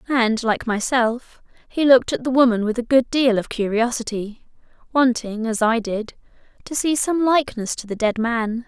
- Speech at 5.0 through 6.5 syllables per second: No, 4.8 syllables/s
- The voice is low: No, high, 240 Hz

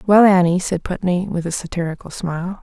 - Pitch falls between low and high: Yes, medium, 180 Hz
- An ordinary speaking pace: Yes, average, 185 wpm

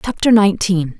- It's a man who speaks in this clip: No, female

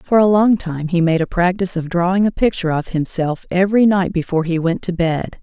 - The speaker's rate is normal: No, fast, 230 wpm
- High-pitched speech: No, medium, 180 Hz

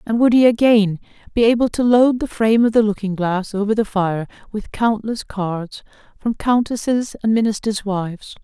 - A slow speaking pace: No, average, 180 wpm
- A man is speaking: No, female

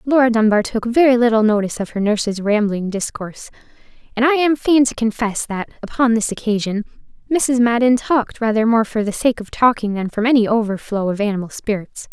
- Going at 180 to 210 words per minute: Yes, average, 190 wpm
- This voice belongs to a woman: Yes, female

